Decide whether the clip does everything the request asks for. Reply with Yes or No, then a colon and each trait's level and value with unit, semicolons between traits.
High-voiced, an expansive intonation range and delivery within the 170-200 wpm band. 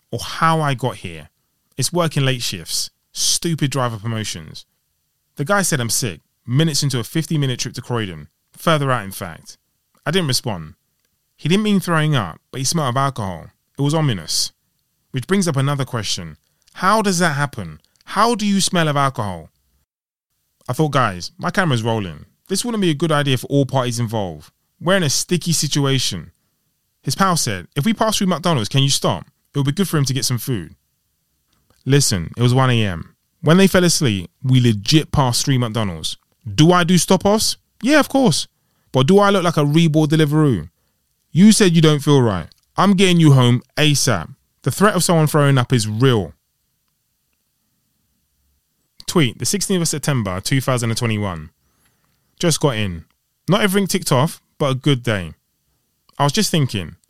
No: low, 135 Hz; wide, 6.8 semitones; average, 180 wpm